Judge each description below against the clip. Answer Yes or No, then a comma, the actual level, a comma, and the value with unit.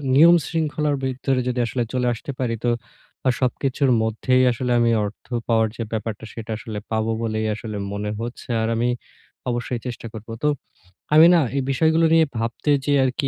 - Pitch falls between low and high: No, low, 120 Hz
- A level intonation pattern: No, average, 3.5 semitones